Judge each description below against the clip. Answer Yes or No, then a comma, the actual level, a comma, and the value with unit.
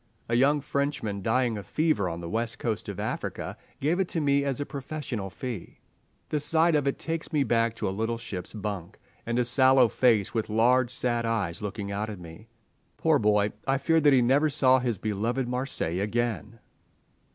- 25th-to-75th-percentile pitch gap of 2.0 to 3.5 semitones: No, average, 4.6 semitones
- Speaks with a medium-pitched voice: No, low, 120 Hz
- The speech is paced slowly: No, average, 195 wpm